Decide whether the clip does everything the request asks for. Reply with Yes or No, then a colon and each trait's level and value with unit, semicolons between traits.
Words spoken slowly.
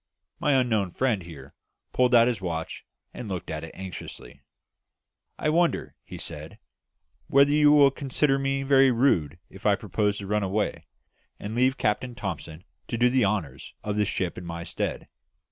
No: average, 170 wpm